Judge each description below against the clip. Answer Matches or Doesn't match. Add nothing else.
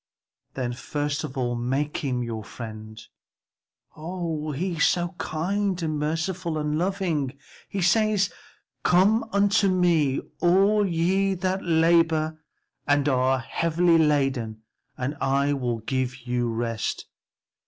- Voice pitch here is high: Doesn't match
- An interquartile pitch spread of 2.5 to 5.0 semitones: Doesn't match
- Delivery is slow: Matches